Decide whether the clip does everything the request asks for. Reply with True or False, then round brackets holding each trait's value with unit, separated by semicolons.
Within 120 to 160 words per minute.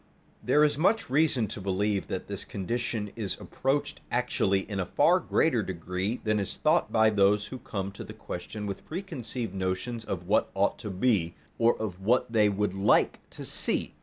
False (185 wpm)